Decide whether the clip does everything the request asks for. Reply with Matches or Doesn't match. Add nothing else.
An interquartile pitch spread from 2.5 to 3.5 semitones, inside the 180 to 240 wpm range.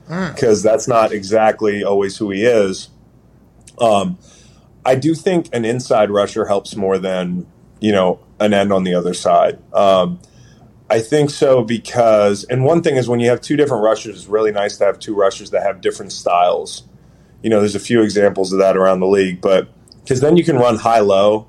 Doesn't match